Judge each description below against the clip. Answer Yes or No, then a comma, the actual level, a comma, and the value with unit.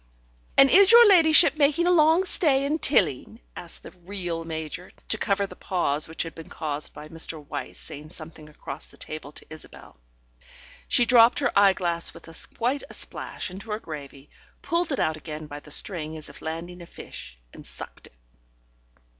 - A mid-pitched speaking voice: Yes, medium, 175 Hz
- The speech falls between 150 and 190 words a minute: Yes, average, 180 wpm